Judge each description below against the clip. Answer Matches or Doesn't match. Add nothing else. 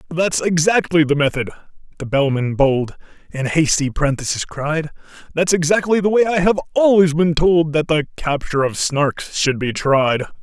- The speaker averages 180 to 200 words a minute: Doesn't match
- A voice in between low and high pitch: Matches